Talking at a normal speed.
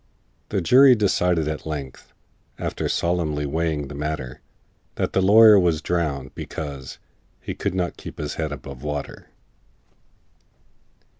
No: slow, 130 wpm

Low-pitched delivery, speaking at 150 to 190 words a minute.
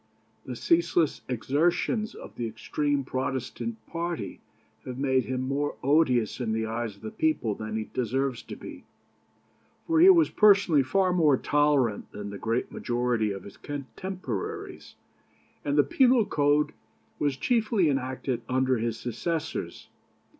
No: low, 130 Hz; average, 140 wpm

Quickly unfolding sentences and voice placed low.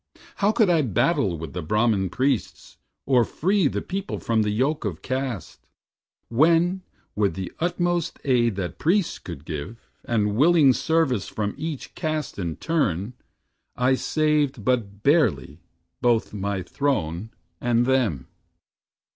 No: slow, 135 wpm; low, 125 Hz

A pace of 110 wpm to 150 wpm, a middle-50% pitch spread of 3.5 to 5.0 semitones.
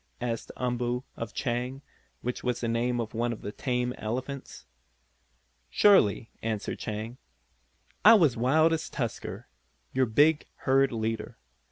No: average, 140 wpm; narrow, 2.6 semitones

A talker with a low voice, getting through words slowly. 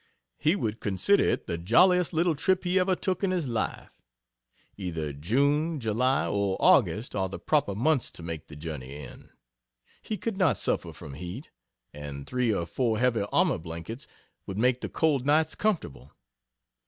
No: low, 120 Hz; average, 165 wpm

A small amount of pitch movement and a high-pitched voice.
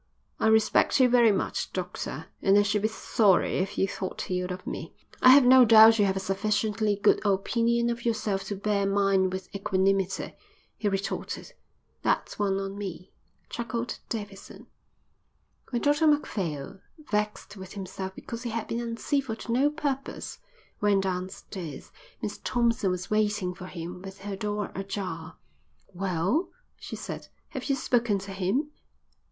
No: average, 3.3 semitones; high, 205 Hz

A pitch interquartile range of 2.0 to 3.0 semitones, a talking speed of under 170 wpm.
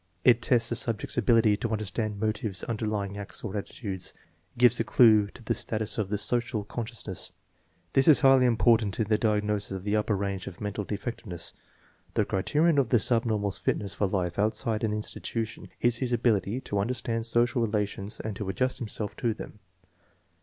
No: narrow, 2.5 semitones; average, 180 wpm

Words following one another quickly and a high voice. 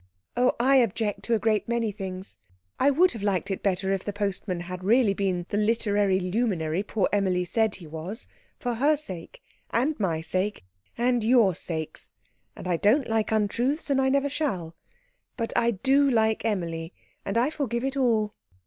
No: average, 175 wpm; high, 210 Hz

